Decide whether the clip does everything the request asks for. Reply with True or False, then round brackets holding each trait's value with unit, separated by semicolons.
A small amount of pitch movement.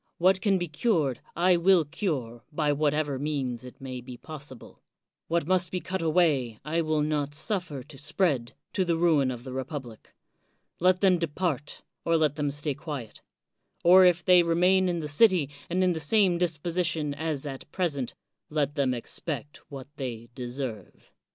False (4.3 semitones)